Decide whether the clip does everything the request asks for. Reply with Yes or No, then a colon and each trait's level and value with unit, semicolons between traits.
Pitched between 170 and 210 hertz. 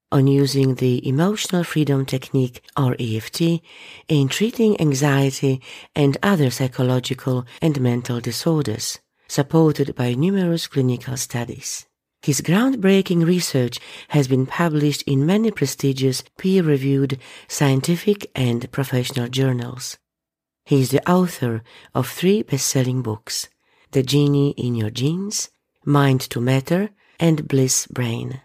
No: medium, 140 Hz